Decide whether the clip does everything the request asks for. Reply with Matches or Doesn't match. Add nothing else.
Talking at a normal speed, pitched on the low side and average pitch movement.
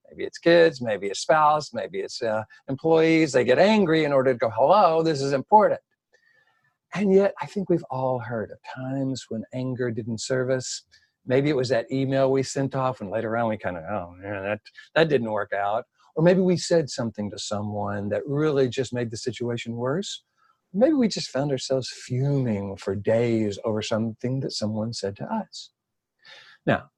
Doesn't match